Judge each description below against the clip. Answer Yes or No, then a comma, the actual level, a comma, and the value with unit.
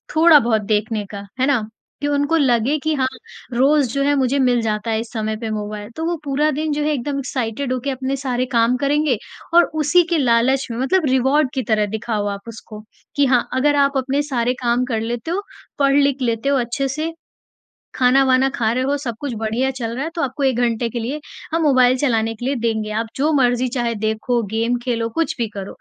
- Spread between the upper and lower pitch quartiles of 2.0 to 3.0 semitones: No, average, 3.5 semitones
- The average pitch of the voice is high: Yes, very high, 255 Hz